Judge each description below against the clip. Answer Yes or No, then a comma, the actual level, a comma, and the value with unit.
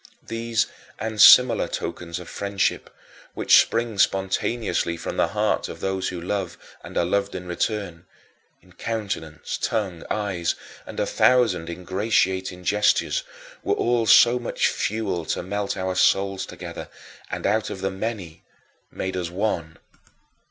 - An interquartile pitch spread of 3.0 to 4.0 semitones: Yes, average, 3.3 semitones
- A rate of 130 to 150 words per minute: Yes, average, 140 wpm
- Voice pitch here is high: No, very low, 95 Hz